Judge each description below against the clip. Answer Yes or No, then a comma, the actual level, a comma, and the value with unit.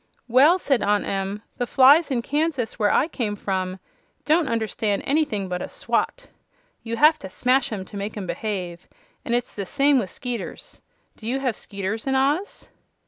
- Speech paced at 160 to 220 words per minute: Yes, average, 185 wpm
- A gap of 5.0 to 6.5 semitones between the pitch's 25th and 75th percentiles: Yes, average, 5.3 semitones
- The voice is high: Yes, high, 230 Hz